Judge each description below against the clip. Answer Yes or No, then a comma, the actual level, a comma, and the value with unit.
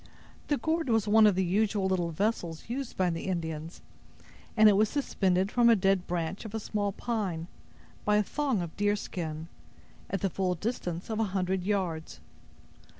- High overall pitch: Yes, high, 195 Hz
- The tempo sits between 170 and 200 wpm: Yes, average, 175 wpm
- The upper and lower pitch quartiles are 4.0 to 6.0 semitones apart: No, average, 3.6 semitones